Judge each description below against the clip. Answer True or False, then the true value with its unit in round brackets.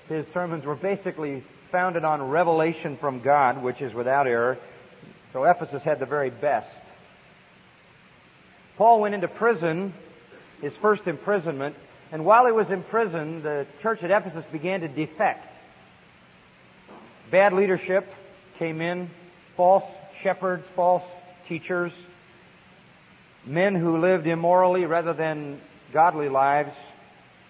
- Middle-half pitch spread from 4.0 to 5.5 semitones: False (3.4 semitones)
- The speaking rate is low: True (120 wpm)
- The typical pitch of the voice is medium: True (175 Hz)